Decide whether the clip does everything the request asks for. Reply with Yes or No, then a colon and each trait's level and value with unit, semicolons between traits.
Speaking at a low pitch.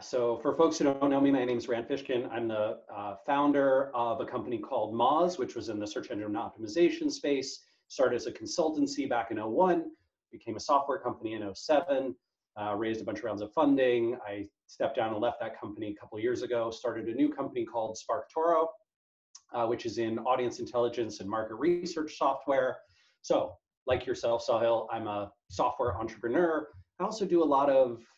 Yes: low, 130 Hz